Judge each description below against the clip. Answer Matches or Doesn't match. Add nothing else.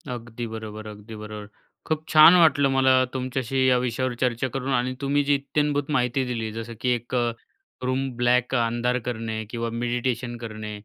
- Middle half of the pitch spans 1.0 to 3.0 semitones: Matches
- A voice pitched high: Doesn't match